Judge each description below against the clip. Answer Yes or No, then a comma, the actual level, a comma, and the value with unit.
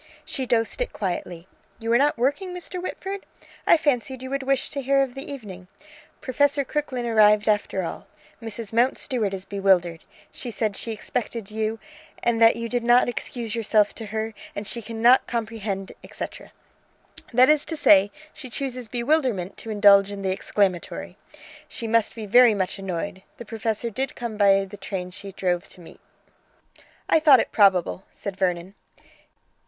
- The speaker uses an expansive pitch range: No, average, 4.2 semitones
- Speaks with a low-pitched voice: No, high, 225 Hz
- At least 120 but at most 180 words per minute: Yes, average, 170 wpm